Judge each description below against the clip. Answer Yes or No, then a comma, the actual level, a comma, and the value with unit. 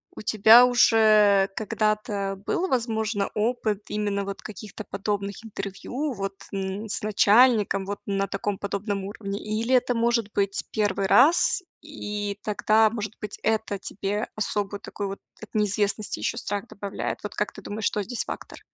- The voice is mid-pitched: No, high, 210 Hz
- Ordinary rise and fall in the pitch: No, narrow, 1.8 semitones